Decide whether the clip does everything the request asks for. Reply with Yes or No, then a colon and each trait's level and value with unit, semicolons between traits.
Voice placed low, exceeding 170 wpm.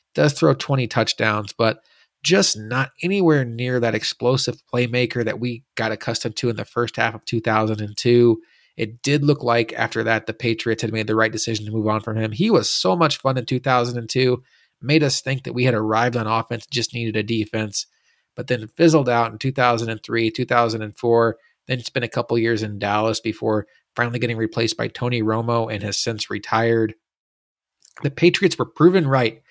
Yes: low, 115 Hz; average, 185 wpm